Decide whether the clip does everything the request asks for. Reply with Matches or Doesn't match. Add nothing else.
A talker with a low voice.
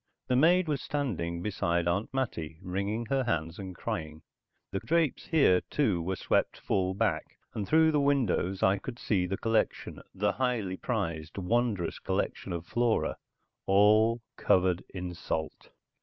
Matches